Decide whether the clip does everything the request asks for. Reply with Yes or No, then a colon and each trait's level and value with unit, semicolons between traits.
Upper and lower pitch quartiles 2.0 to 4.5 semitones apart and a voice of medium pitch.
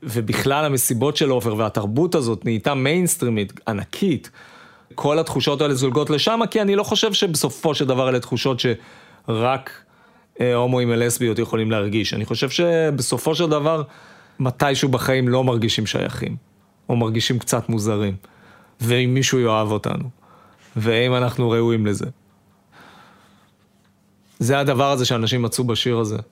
No: average, 4.0 semitones; low, 125 Hz